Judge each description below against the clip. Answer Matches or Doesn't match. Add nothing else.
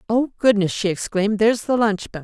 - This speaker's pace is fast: Matches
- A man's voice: Doesn't match